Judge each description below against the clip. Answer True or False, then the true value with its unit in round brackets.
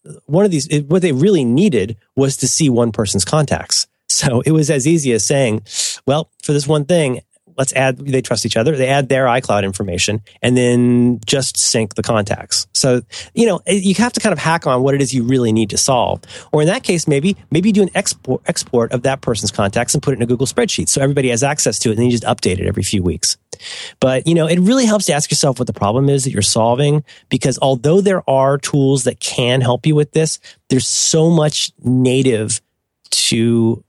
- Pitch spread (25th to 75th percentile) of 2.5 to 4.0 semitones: False (4.6 semitones)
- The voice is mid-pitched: False (130 Hz)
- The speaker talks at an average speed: False (225 wpm)